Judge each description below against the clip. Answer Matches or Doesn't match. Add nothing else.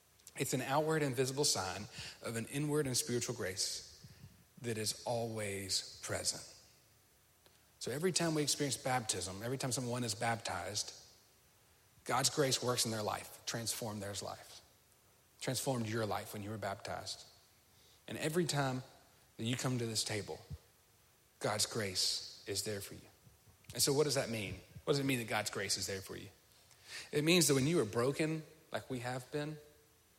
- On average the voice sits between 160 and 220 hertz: Doesn't match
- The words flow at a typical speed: Matches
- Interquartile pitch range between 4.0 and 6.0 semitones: Matches